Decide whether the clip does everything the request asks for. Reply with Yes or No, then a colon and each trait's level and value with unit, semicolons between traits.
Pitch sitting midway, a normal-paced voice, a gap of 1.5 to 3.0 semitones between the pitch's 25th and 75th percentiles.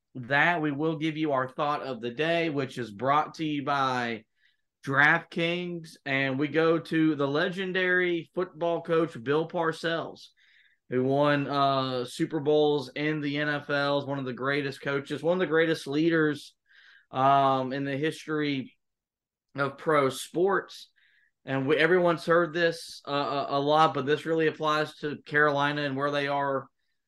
Yes: medium, 150 Hz; average, 155 wpm; average, 2.7 semitones